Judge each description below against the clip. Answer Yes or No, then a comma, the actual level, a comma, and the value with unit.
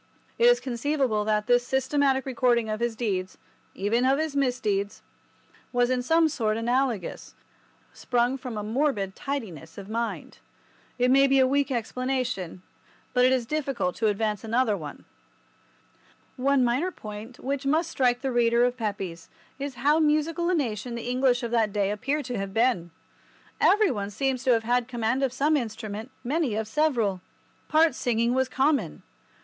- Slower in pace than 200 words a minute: Yes, average, 160 wpm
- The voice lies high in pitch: Yes, high, 245 Hz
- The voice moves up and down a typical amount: Yes, average, 3.9 semitones